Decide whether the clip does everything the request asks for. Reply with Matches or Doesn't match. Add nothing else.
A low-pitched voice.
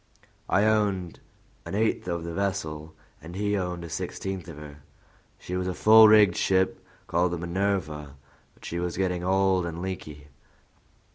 Matches